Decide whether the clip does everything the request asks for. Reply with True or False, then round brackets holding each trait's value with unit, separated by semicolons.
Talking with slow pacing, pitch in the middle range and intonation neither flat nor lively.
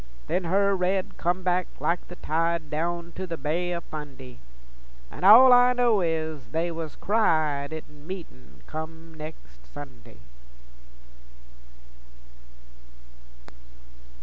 True (115 wpm; 165 Hz; 3.2 semitones)